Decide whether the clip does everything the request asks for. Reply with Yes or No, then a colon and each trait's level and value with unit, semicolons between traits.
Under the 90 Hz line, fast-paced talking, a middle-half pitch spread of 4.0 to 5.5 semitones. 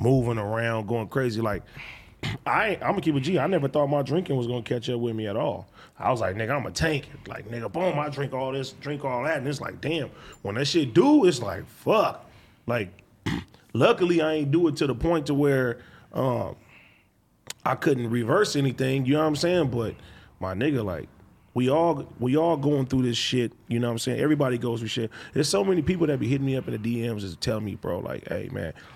No: low, 135 Hz; fast, 230 wpm; average, 4.3 semitones